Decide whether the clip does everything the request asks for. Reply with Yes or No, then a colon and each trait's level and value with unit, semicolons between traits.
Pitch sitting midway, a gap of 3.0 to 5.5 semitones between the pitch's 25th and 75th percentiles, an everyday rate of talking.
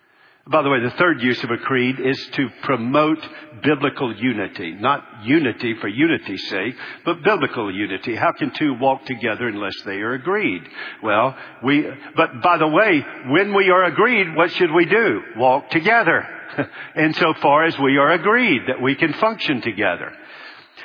Yes: medium, 150 Hz; average, 5.1 semitones; average, 170 wpm